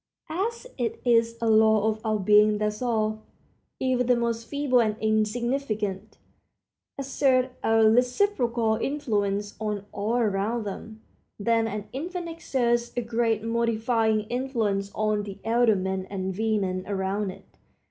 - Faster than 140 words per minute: No, slow, 135 wpm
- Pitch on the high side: Yes, high, 220 Hz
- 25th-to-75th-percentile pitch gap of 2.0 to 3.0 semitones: Yes, narrow, 2.4 semitones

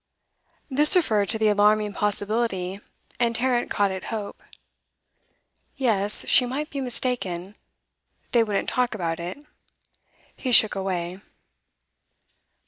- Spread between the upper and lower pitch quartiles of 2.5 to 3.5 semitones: No, average, 4.0 semitones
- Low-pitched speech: No, high, 215 Hz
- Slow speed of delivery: Yes, slow, 120 wpm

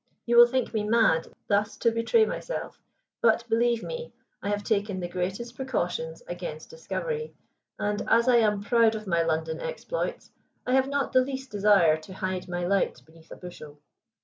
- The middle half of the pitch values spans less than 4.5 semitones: No, average, 5.1 semitones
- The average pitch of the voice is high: Yes, high, 215 Hz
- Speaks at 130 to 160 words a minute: No, average, 175 wpm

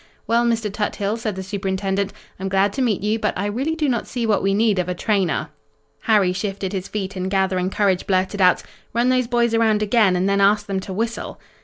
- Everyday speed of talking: No, fast, 220 wpm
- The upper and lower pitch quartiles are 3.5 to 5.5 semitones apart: No, average, 2.9 semitones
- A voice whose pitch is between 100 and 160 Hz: No, high, 200 Hz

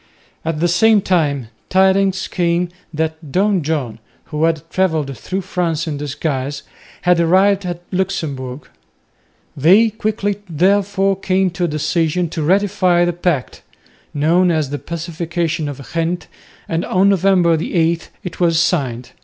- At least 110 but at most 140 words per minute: Yes, slow, 135 wpm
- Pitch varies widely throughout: No, average, 3.3 semitones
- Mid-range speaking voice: Yes, medium, 170 Hz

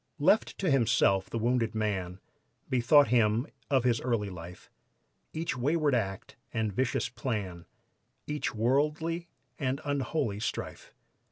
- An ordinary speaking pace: No, slow, 120 wpm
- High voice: No, low, 120 Hz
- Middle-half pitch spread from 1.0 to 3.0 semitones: No, average, 5.1 semitones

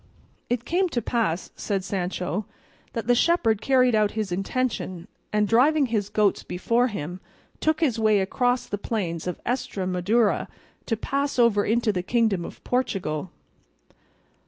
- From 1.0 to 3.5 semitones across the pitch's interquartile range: No, average, 4.4 semitones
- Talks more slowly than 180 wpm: Yes, average, 145 wpm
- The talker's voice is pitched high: Yes, high, 220 Hz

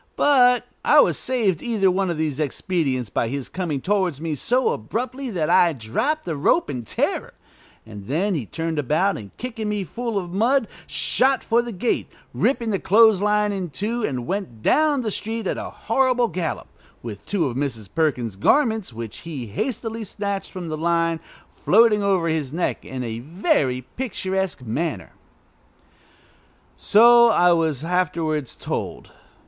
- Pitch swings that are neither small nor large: No, wide, 7.2 semitones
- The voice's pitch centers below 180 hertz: No, medium, 185 Hz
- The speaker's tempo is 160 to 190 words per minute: Yes, average, 165 wpm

